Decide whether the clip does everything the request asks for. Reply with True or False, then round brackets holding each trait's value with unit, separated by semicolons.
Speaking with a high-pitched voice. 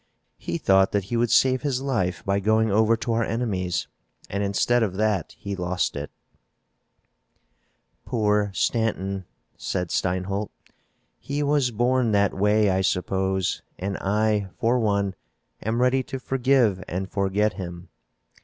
False (105 Hz)